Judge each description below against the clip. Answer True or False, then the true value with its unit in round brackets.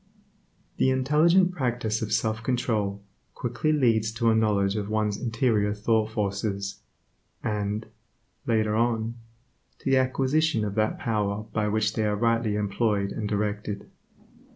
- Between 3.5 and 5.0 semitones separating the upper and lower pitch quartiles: False (2.5 semitones)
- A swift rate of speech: False (135 wpm)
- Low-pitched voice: True (110 Hz)